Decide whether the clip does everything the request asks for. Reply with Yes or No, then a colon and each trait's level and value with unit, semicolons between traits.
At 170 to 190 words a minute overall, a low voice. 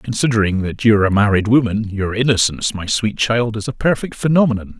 No: average, 200 wpm; low, 110 Hz